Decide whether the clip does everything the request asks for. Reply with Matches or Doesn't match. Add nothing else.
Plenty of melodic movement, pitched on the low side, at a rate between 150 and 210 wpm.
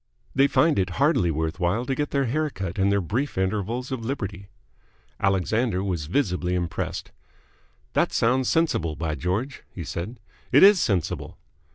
Matches